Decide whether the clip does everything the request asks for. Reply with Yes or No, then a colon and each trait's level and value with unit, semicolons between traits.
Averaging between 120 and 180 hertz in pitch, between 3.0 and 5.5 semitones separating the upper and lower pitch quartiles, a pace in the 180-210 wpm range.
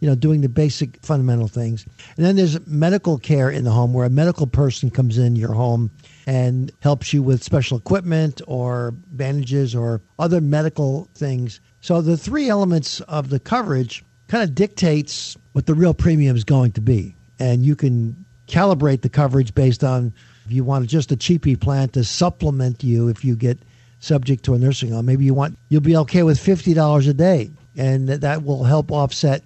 Yes: medium, 140 Hz; average, 3.6 semitones; average, 195 wpm